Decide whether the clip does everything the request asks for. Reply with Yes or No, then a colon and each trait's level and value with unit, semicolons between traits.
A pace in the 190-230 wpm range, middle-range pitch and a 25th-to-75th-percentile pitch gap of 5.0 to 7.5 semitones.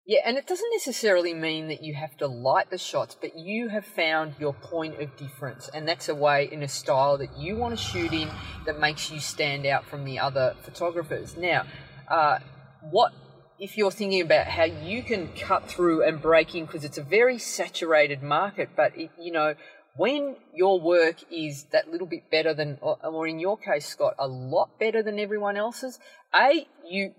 Yes: average, 200 wpm; medium, 160 Hz; wide, 5.6 semitones